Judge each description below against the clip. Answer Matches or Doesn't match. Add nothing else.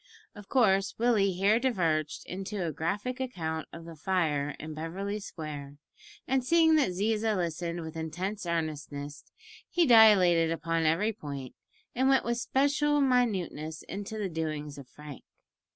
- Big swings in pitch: Matches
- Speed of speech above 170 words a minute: Doesn't match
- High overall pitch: Doesn't match